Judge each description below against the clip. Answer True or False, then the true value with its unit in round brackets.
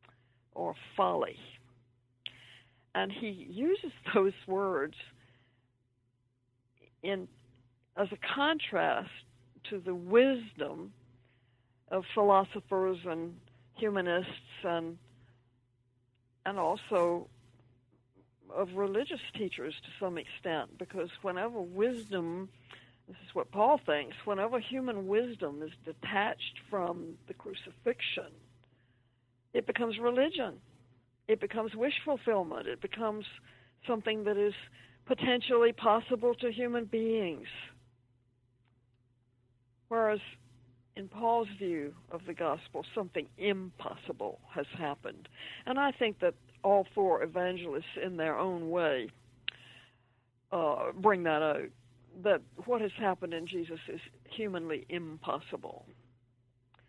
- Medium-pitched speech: True (165 Hz)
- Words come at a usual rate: False (100 wpm)